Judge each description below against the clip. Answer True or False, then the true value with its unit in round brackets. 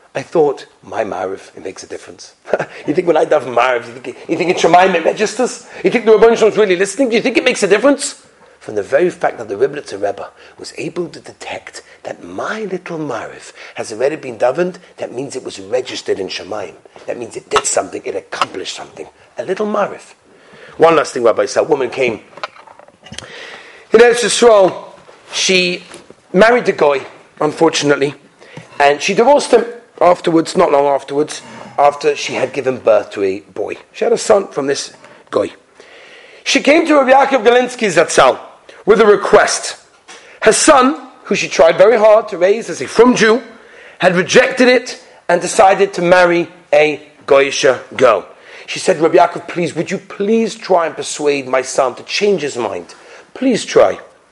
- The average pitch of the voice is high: True (215 Hz)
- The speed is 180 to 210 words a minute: True (185 wpm)